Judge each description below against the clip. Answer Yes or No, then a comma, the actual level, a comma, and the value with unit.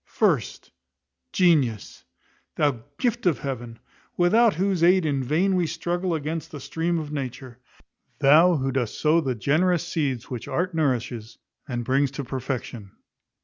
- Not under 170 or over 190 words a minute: No, average, 145 wpm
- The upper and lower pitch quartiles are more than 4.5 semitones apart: Yes, average, 5.1 semitones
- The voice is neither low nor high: Yes, medium, 150 Hz